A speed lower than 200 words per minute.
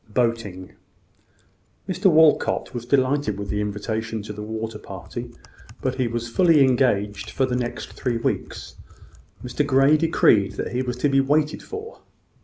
Yes: average, 150 wpm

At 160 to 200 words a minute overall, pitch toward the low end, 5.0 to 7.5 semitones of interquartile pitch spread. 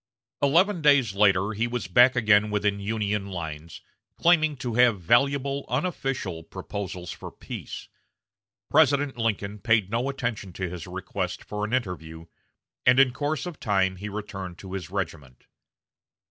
No: average, 145 wpm; low, 105 Hz; wide, 5.5 semitones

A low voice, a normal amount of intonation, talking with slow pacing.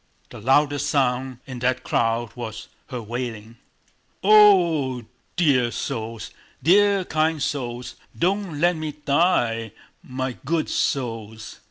Yes: low, 130 Hz; average, 5.0 semitones; slow, 125 wpm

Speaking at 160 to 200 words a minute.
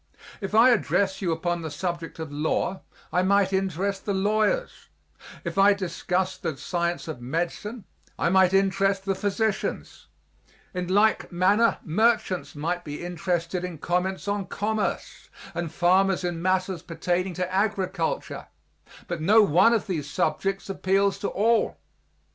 No: average, 140 wpm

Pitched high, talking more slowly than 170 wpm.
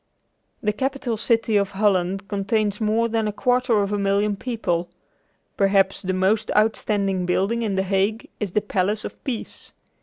Yes: high, 210 Hz; average, 160 wpm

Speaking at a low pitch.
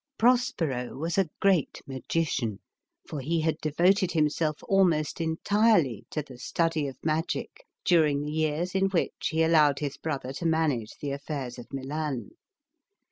No: medium, 155 Hz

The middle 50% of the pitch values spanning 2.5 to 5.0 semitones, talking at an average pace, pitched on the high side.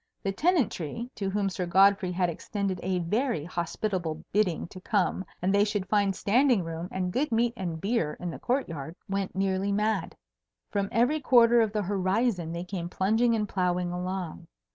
Yes: average, 3.4 semitones; average, 180 wpm; high, 195 Hz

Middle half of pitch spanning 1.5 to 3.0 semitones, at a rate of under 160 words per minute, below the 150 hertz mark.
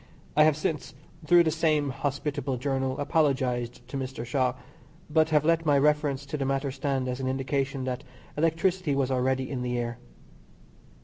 No: narrow, 2.5 semitones; average, 170 wpm; medium, 140 Hz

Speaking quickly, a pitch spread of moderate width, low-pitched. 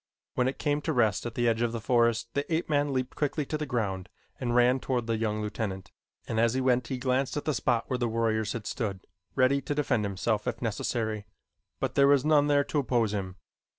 Yes: fast, 230 wpm; average, 3.8 semitones; low, 120 Hz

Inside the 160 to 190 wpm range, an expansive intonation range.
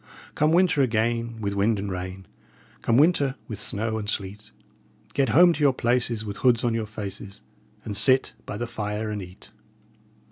No: average, 175 wpm; average, 3.6 semitones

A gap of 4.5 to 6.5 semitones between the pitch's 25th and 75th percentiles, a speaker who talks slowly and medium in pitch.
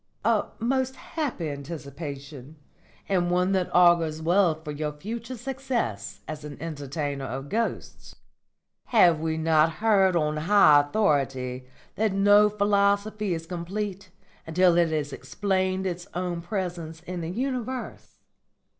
Yes: average, 4.9 semitones; slow, 130 wpm; medium, 175 Hz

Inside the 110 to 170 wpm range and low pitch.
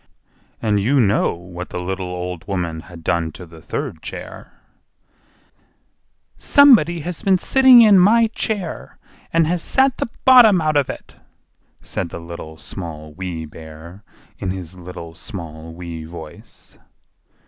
Yes: average, 140 wpm; very low, 90 Hz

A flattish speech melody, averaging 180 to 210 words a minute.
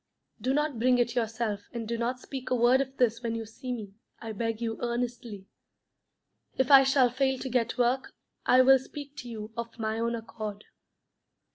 Yes: narrow, 2.2 semitones; average, 190 wpm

